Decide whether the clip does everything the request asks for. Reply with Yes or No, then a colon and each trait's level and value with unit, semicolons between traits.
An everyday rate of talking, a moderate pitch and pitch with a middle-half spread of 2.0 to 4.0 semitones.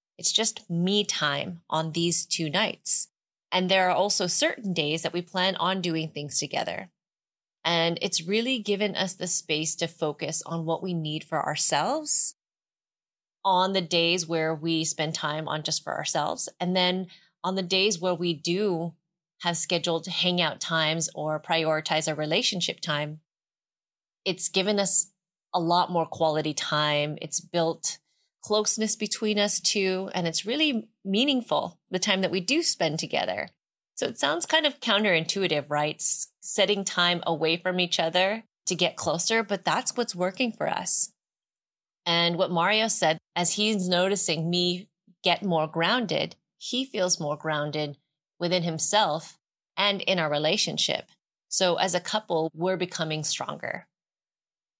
Yes: average, 150 wpm; medium, 175 Hz; average, 3.3 semitones